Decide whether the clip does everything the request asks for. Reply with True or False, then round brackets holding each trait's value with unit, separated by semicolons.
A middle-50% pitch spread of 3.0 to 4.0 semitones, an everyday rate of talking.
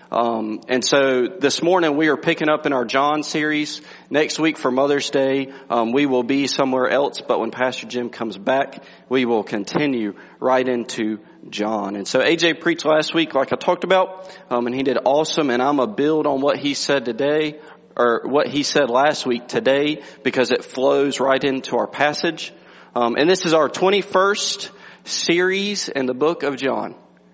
True (3.5 semitones; 185 wpm)